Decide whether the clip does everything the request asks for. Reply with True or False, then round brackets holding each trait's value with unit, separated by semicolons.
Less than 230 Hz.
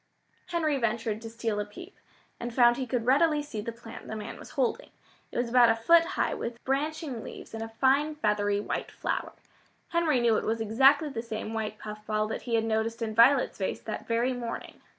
False (235 Hz)